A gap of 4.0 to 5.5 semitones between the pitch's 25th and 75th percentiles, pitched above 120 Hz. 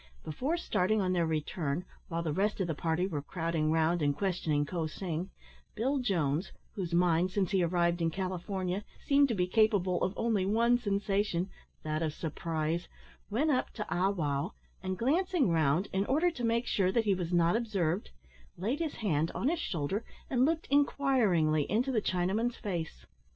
Yes: average, 5.1 semitones; medium, 185 Hz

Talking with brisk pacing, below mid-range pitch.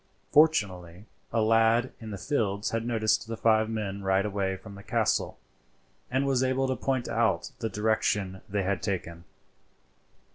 No: average, 155 wpm; low, 110 Hz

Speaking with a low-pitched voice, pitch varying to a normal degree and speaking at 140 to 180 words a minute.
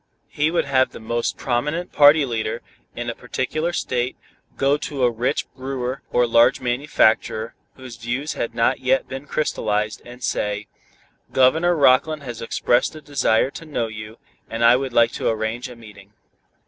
Yes: low, 125 Hz; average, 3.0 semitones; average, 165 wpm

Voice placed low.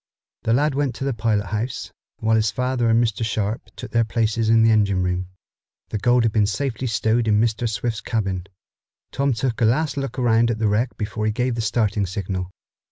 Yes: low, 115 Hz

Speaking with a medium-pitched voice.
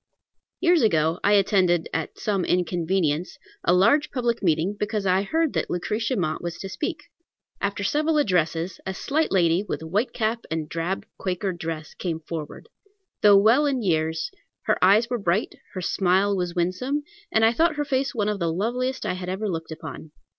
No: high, 195 Hz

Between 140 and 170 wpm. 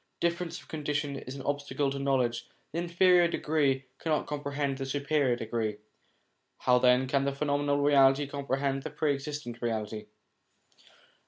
Yes: average, 145 wpm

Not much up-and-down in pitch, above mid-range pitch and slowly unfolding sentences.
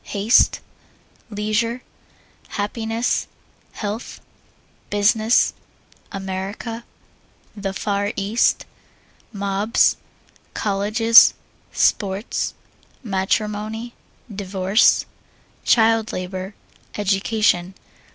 Yes: narrow, 2.3 semitones; high, 210 Hz; slow, 55 wpm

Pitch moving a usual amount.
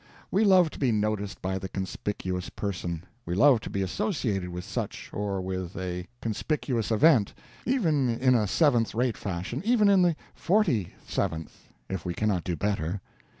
No: wide, 7.5 semitones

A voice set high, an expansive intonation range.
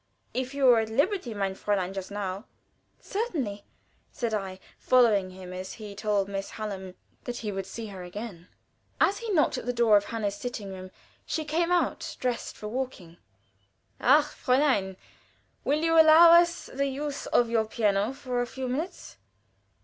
Yes: high, 230 Hz; wide, 5.8 semitones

